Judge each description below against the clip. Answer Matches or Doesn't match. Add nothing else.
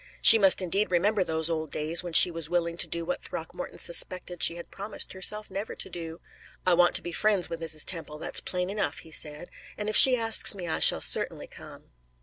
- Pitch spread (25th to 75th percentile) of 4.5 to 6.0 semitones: Doesn't match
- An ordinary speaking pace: Doesn't match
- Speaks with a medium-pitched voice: Matches